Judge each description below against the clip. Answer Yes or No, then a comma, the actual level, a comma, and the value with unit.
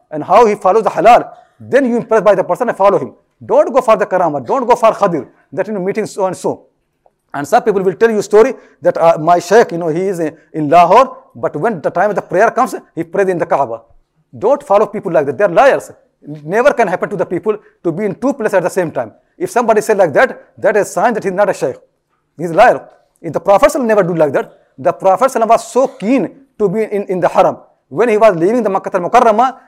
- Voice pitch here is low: No, high, 205 Hz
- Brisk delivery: Yes, fast, 265 wpm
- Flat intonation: No, average, 4.7 semitones